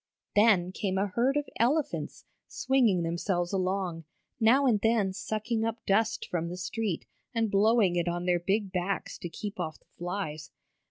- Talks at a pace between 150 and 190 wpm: Yes, average, 165 wpm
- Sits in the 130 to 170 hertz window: No, high, 195 Hz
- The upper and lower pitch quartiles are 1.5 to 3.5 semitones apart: No, average, 4.2 semitones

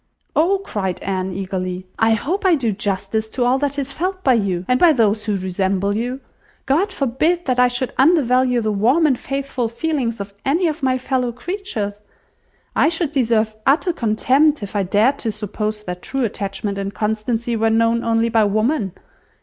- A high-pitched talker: Yes, high, 230 Hz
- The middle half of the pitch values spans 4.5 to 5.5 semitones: Yes, average, 4.8 semitones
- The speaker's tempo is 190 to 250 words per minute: No, average, 180 wpm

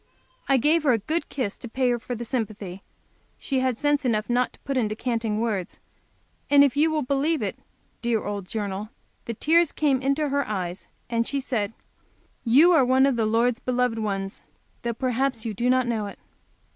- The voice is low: No, high, 245 Hz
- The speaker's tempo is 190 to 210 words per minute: Yes, average, 195 wpm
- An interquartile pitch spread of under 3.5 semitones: No, average, 4.0 semitones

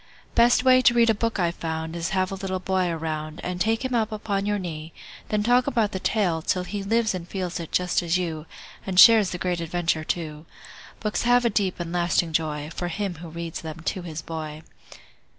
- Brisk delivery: Yes, fast, 220 wpm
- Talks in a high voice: No, medium, 180 Hz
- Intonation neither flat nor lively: Yes, average, 4.2 semitones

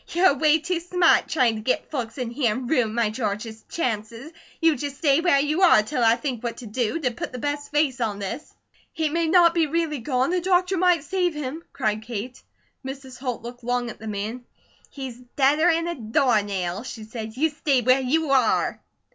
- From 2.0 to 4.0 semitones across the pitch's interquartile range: No, wide, 5.4 semitones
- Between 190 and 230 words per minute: Yes, fast, 205 wpm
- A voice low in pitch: No, very high, 260 Hz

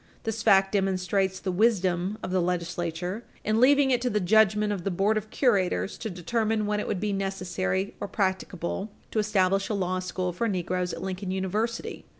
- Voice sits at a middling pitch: No, high, 195 Hz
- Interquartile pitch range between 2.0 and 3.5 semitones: Yes, narrow, 2.6 semitones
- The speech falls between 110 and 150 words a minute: No, average, 185 wpm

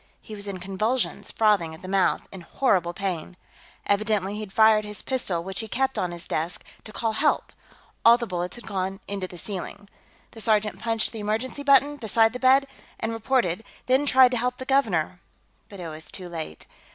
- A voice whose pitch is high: Yes, high, 210 Hz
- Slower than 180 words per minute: No, average, 195 wpm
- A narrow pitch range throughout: No, average, 4.3 semitones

